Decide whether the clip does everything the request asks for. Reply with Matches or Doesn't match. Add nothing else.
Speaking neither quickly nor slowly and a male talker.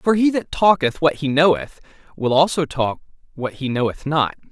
Matches